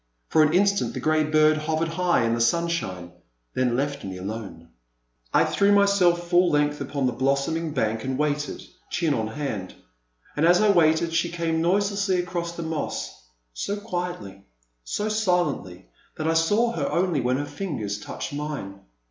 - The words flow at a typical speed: Yes, average, 170 wpm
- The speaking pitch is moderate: Yes, medium, 155 Hz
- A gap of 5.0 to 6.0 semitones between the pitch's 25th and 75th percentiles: Yes, wide, 5.4 semitones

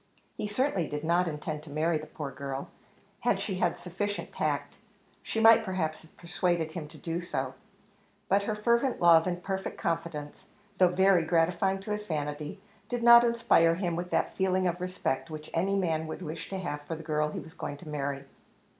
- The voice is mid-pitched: Yes, medium, 170 Hz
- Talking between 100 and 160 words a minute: No, average, 195 wpm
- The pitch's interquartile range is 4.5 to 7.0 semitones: No, average, 3.7 semitones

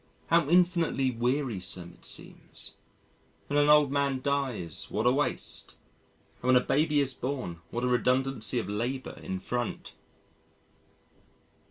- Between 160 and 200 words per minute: No, slow, 135 wpm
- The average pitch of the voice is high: No, low, 130 Hz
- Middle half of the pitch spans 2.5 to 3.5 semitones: Yes, average, 2.9 semitones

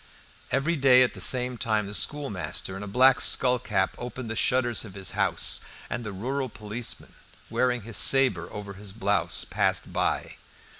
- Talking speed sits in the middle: Yes, average, 165 wpm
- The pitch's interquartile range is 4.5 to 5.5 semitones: No, average, 3.8 semitones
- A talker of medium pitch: No, low, 115 Hz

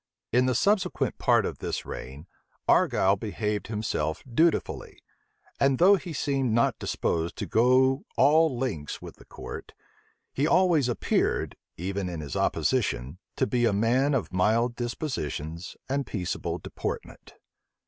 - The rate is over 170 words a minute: No, average, 140 wpm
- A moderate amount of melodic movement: No, wide, 6.4 semitones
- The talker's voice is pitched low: Yes, low, 120 Hz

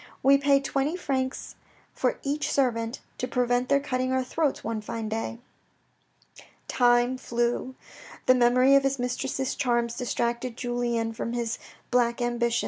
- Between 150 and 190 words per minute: No, average, 140 wpm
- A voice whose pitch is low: No, high, 245 Hz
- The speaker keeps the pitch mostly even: Yes, narrow, 1.9 semitones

